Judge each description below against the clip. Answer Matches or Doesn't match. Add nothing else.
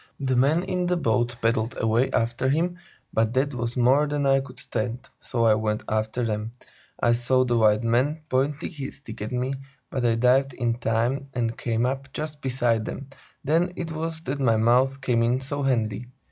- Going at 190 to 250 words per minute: Matches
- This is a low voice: Matches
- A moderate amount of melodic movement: Matches